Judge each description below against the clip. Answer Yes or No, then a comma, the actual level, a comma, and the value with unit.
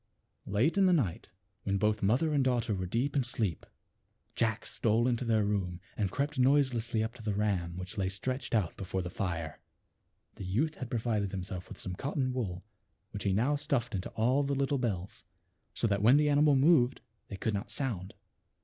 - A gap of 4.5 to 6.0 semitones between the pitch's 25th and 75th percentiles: Yes, average, 5.2 semitones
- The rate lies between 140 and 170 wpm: No, average, 195 wpm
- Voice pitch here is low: Yes, low, 110 Hz